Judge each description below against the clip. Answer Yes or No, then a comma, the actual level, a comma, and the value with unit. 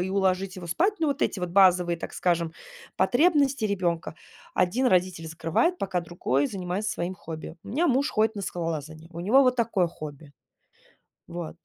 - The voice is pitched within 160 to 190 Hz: Yes, medium, 185 Hz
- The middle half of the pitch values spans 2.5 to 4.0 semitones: No, average, 4.6 semitones